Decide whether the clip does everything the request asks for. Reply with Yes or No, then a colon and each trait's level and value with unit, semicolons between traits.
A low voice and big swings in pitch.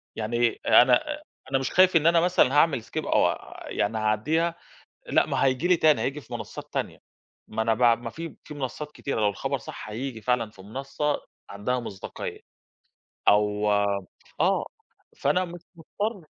Yes: low, 130 Hz; wide, 6.6 semitones